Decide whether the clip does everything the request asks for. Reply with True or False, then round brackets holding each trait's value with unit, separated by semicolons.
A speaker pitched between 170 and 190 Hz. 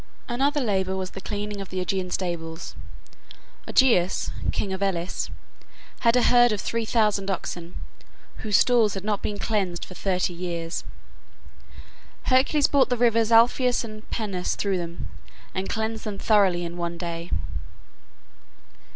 False (200 Hz)